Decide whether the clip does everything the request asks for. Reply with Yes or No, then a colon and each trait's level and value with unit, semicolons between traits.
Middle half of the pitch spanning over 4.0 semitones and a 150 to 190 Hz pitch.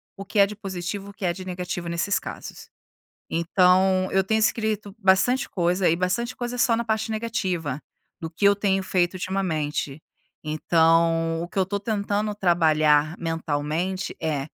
No: average, 3.5 semitones; medium, 185 Hz